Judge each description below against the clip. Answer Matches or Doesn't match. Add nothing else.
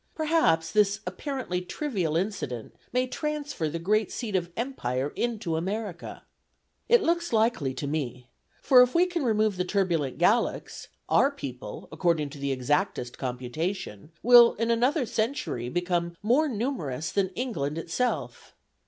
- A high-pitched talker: Matches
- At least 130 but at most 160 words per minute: Matches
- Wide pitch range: Matches